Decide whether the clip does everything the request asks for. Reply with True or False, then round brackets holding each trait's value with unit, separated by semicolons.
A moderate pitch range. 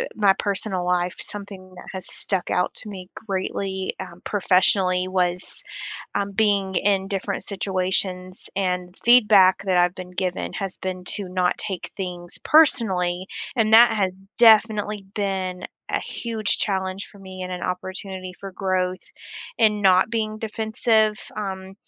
False (2.1 semitones)